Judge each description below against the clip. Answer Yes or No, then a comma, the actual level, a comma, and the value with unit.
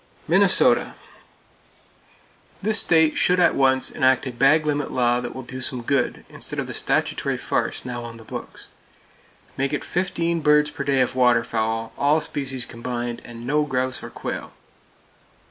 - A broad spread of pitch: No, average, 3.7 semitones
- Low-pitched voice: Yes, low, 130 Hz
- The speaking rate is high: No, average, 160 wpm